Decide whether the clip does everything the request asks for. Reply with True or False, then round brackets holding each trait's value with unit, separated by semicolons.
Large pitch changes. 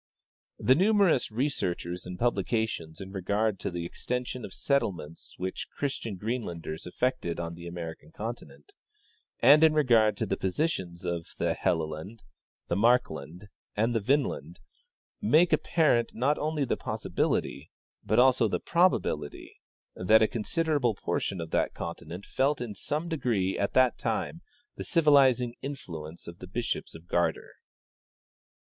True (7.2 semitones)